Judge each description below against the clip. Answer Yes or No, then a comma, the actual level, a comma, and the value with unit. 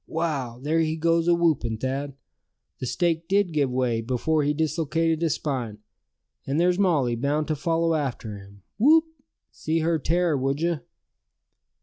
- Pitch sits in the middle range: Yes, medium, 155 Hz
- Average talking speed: Yes, average, 150 wpm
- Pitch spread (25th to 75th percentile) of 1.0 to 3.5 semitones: No, average, 4.0 semitones